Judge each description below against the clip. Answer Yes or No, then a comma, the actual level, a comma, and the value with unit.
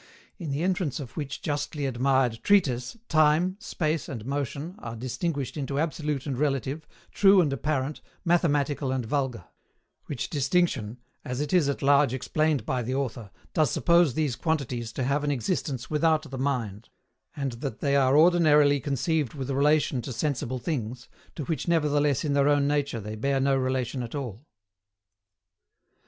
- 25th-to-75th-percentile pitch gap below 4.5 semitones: Yes, average, 2.9 semitones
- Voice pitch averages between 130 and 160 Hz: Yes, medium, 140 Hz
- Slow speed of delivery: No, average, 160 wpm